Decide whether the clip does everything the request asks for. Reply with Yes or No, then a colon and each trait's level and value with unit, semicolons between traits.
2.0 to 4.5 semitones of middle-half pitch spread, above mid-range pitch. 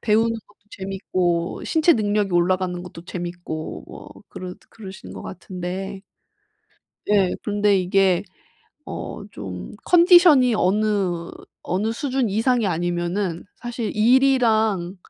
Yes: average, 4.0 semitones; high, 195 Hz